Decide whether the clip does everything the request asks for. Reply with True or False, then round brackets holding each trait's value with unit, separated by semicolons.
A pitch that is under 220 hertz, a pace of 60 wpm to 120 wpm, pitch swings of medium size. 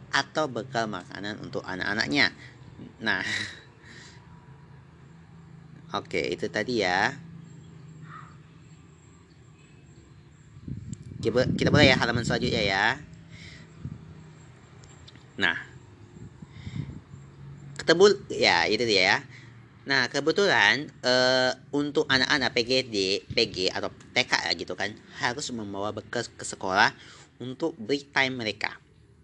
True (140 Hz; 90 wpm; 3.9 semitones)